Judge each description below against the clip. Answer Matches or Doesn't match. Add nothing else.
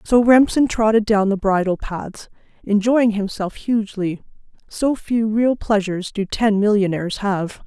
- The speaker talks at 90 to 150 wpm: Matches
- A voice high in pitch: Matches